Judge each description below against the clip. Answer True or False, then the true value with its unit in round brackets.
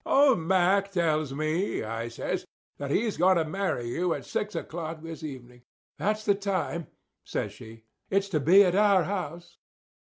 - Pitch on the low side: False (175 Hz)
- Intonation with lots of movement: False (4.4 semitones)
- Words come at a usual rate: True (165 wpm)